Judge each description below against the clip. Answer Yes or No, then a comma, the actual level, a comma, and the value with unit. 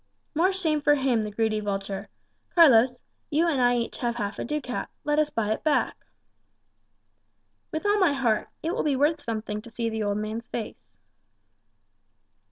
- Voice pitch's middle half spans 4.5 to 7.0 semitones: Yes, wide, 5.6 semitones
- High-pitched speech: Yes, high, 245 Hz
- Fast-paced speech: No, average, 175 wpm